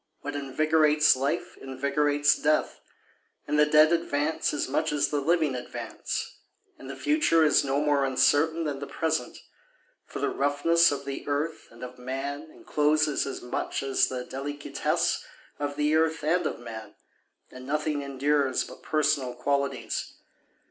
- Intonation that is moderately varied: No, narrow, 2.1 semitones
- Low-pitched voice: No, medium, 145 Hz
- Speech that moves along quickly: No, average, 150 wpm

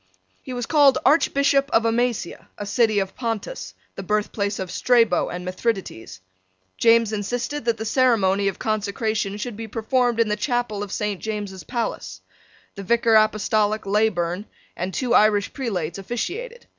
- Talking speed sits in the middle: Yes, average, 150 wpm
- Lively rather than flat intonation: No, average, 3.1 semitones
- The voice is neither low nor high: No, high, 220 Hz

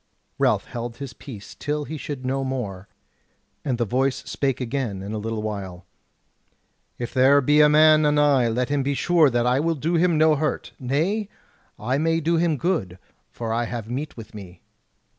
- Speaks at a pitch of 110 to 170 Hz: Yes, low, 135 Hz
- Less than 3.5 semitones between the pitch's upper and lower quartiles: No, average, 4.4 semitones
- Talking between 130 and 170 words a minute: No, average, 185 wpm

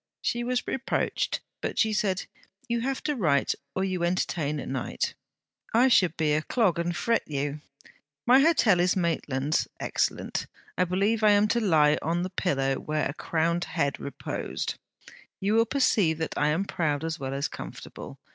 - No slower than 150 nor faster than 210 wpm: Yes, average, 175 wpm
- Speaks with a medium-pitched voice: Yes, medium, 175 Hz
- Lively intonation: Yes, wide, 6.0 semitones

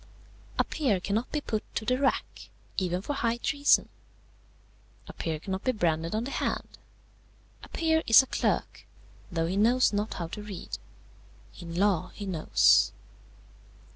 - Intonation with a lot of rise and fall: Yes, wide, 5.9 semitones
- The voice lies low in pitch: No, high, 210 Hz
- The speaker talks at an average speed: Yes, average, 155 wpm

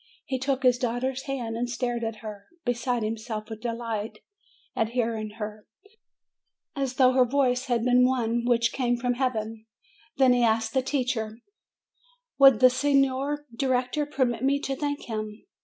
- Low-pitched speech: No, high, 245 Hz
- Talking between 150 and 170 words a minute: Yes, average, 160 wpm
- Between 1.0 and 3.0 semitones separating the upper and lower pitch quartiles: Yes, narrow, 2.6 semitones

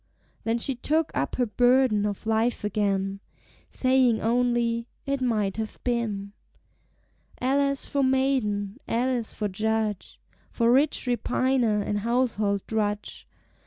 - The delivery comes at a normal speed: No, slow, 120 wpm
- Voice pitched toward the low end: No, high, 230 Hz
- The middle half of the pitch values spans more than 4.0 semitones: No, average, 3.5 semitones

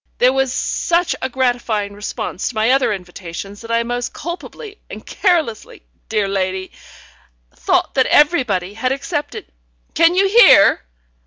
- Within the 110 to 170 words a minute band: Yes, average, 140 wpm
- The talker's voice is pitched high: Yes, high, 245 Hz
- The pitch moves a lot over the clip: Yes, wide, 6.4 semitones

